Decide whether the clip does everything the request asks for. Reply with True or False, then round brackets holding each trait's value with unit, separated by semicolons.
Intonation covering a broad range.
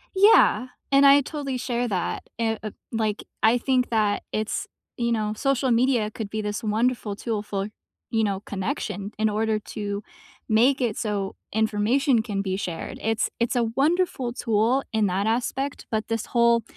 False (3.0 semitones)